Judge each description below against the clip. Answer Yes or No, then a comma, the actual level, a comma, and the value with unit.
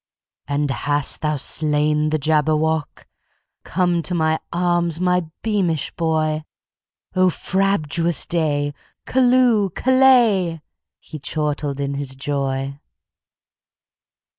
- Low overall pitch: No, medium, 155 Hz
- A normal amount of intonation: Yes, average, 3.7 semitones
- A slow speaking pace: Yes, slow, 85 wpm